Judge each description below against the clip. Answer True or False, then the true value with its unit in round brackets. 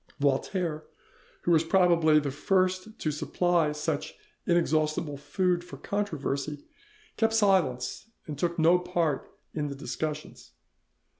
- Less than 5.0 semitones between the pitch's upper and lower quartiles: True (3.2 semitones)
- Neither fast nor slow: False (120 wpm)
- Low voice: False (160 Hz)